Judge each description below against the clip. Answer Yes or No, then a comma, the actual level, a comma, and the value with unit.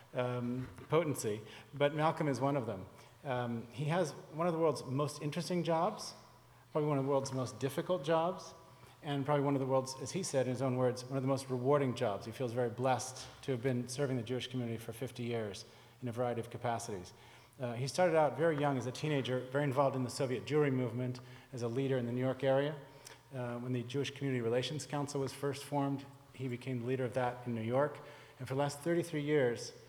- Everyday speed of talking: No, fast, 225 wpm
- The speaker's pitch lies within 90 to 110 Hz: No, low, 130 Hz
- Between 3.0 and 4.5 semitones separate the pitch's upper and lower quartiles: No, narrow, 2.6 semitones